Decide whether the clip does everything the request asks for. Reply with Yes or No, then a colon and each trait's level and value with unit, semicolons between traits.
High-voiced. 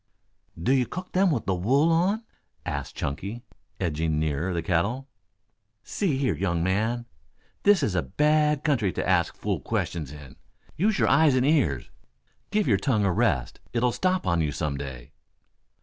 No: low, 110 Hz